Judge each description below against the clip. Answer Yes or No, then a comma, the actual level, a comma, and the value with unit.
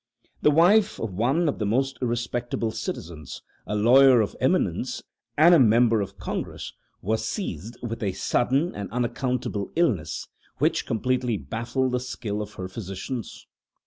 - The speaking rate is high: No, average, 145 wpm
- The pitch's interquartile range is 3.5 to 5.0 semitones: Yes, average, 3.9 semitones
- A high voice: No, low, 120 Hz